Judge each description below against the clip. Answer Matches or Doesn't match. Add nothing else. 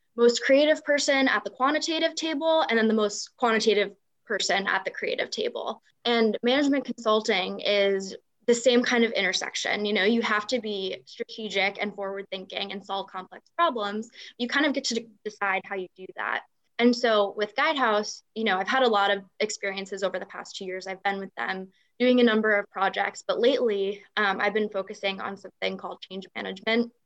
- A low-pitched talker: Doesn't match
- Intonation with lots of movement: Doesn't match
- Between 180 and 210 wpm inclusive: Matches